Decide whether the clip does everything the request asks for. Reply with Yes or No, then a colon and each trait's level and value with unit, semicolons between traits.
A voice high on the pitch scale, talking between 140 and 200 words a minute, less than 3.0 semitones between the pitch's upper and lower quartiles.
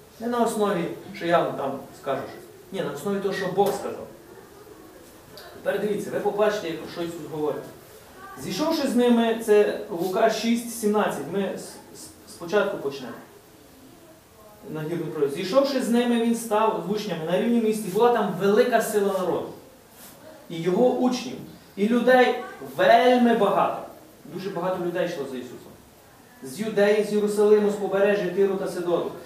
No: high, 205 Hz; average, 145 wpm; average, 4.1 semitones